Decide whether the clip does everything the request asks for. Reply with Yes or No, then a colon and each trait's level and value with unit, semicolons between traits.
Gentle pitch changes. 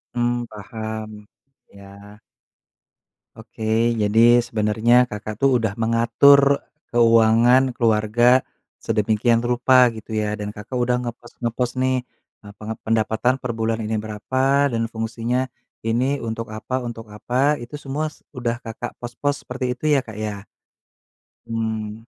Yes: narrow, 2.3 semitones